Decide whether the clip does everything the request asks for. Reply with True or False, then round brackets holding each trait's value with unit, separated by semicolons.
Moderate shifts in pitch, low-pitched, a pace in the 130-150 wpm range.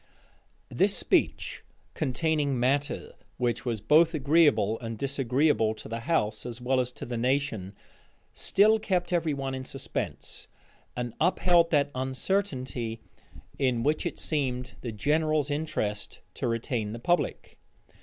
True (4.7 semitones; 130 Hz; 135 wpm)